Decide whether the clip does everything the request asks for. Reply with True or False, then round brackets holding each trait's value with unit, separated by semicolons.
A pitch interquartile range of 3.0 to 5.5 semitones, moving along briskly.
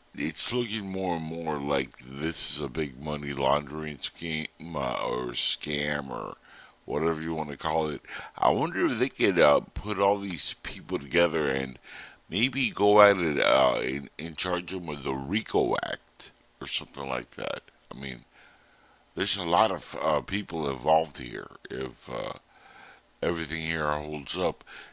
False (3.4 semitones; 160 wpm)